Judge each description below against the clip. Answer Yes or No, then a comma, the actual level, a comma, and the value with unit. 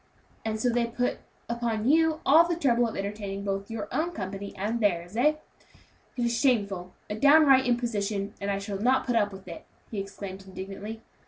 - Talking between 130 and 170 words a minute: No, average, 185 wpm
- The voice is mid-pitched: No, high, 220 Hz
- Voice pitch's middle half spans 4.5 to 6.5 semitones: No, average, 3.7 semitones